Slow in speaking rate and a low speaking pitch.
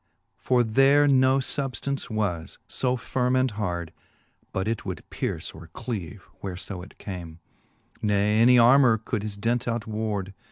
No: average, 155 wpm; low, 110 Hz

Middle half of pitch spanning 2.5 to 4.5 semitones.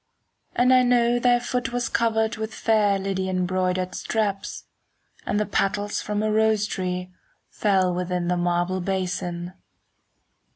Yes: average, 3.3 semitones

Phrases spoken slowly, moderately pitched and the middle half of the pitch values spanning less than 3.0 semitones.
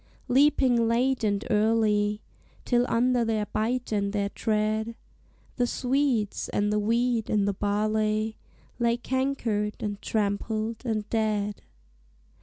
No: slow, 120 wpm; high, 220 Hz; narrow, 2.4 semitones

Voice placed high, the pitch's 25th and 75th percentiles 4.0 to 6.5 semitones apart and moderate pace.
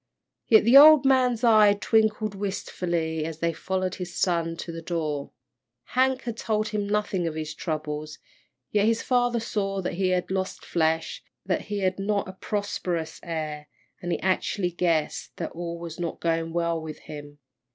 No: medium, 180 Hz; average, 4.3 semitones; average, 170 wpm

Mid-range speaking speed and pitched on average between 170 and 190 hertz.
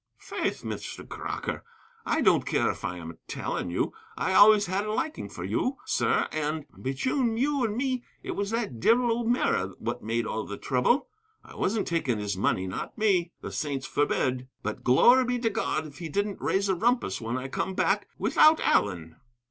Yes: average, 190 wpm; medium, 185 Hz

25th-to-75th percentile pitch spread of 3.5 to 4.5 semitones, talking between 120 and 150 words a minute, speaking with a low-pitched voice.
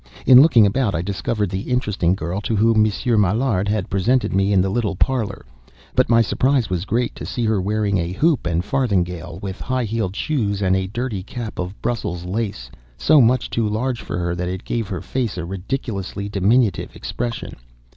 No: average, 4.1 semitones; average, 195 wpm; low, 105 Hz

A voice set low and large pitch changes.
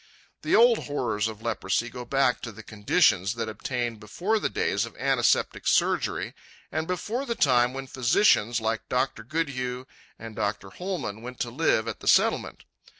No: low, 120 Hz; average, 4.4 semitones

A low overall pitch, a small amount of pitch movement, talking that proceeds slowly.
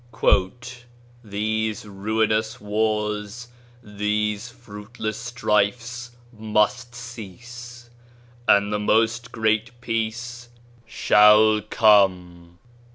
Yes: low, 110 Hz; narrow, 2.3 semitones; slow, 75 wpm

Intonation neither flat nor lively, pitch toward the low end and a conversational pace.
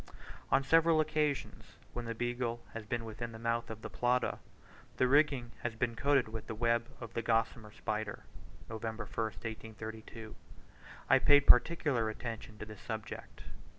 No: narrow, 2.2 semitones; low, 115 Hz; average, 165 wpm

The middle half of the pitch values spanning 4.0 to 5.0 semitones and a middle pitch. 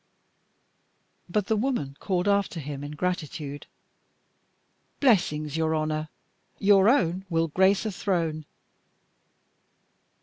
Yes: average, 4.5 semitones; medium, 175 Hz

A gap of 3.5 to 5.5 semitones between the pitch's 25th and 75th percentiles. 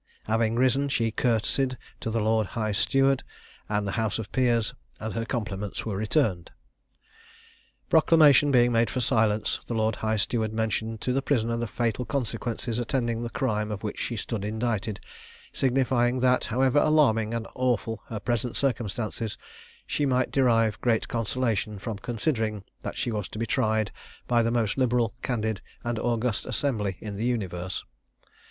No: narrow, 2.4 semitones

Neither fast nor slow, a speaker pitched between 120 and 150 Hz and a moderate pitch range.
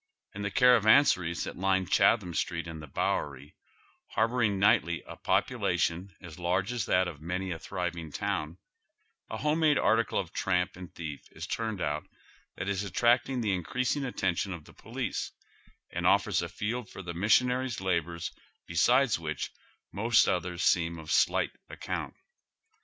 No: average, 160 wpm; very low, 95 Hz; average, 4.9 semitones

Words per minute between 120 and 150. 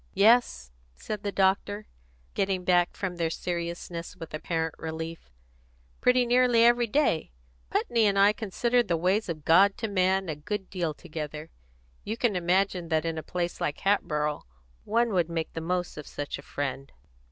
No: average, 165 wpm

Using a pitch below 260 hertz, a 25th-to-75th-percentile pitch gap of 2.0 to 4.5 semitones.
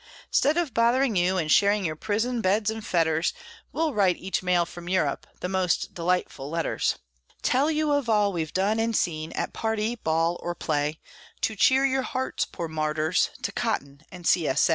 No: medium, 185 Hz; wide, 5.4 semitones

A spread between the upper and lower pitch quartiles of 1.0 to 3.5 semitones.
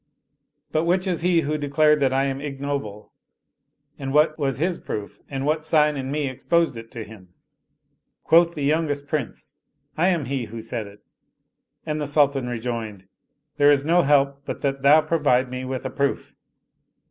Yes: average, 3.1 semitones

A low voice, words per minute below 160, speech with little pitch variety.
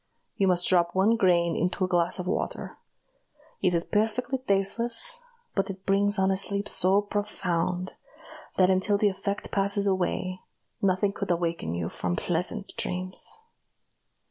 No: high, 190 Hz; average, 145 wpm; narrow, 2.2 semitones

